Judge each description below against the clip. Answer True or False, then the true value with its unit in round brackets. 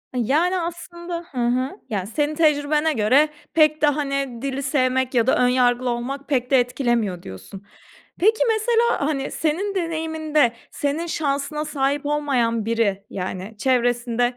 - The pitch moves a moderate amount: True (4.1 semitones)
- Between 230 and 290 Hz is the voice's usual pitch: True (275 Hz)